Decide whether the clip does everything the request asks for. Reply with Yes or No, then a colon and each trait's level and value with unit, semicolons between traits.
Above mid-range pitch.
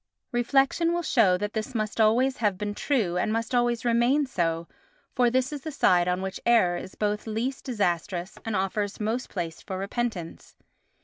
Yes: high, 220 Hz